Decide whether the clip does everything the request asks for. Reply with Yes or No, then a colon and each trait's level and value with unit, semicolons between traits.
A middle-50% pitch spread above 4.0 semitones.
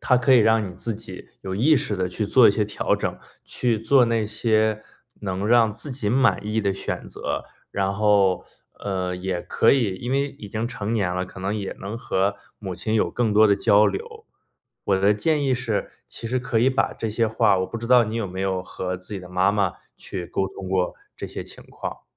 No: average, 3.3 semitones